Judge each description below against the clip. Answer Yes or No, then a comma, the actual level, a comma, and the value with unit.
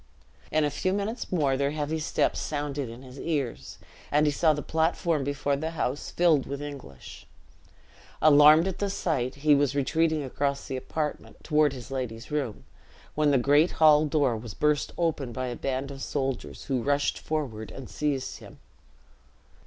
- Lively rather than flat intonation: No, narrow, 2.5 semitones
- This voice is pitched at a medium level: Yes, medium, 145 Hz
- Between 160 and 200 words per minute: Yes, average, 170 wpm